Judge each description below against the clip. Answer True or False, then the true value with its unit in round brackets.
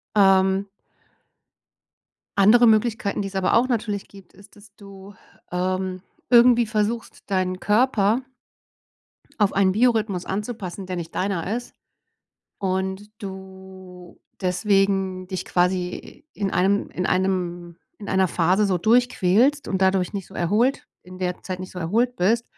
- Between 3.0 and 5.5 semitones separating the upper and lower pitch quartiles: False (2.5 semitones)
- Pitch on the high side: True (195 Hz)